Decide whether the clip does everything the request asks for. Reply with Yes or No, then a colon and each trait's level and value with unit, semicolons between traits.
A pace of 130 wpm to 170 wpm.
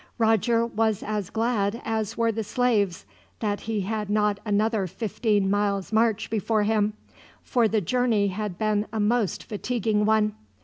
Yes: average, 150 wpm